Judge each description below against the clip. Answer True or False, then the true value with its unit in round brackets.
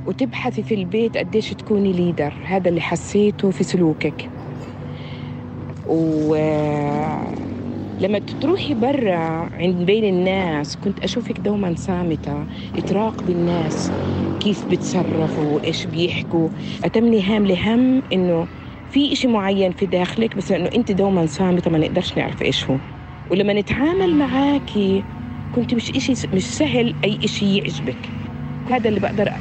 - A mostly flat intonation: False (5.0 semitones)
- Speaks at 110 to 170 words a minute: True (125 wpm)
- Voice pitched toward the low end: False (185 Hz)